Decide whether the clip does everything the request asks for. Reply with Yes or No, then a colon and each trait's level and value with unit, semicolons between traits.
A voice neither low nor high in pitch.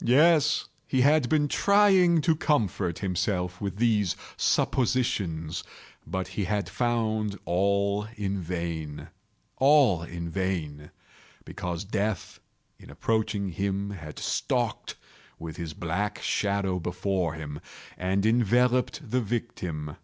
No: low, 100 Hz